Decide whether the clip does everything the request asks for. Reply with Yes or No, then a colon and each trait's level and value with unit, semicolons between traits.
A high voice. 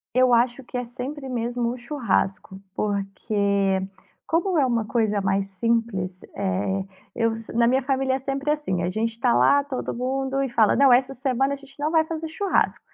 Yes: high, 240 Hz